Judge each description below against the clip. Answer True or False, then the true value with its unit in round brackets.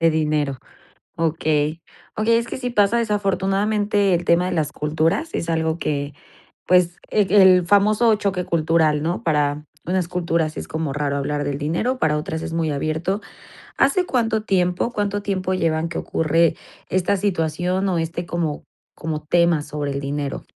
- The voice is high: False (170 Hz)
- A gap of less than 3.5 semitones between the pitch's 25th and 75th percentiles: False (4.1 semitones)